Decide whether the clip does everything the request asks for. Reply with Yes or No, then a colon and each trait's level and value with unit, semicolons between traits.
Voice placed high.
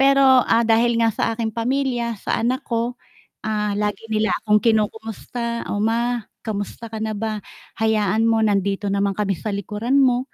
Yes: high, 225 Hz